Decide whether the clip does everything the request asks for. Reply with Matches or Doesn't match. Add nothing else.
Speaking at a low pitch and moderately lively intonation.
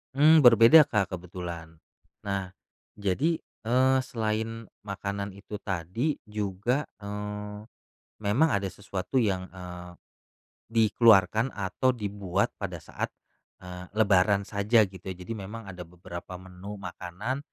Matches